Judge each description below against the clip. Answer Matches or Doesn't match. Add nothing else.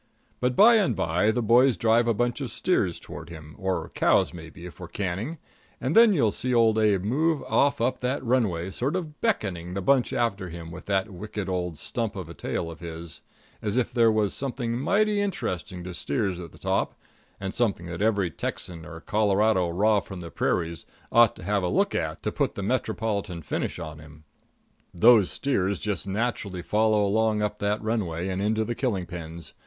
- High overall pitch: Doesn't match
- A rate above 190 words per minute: Matches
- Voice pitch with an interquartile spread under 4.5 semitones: Doesn't match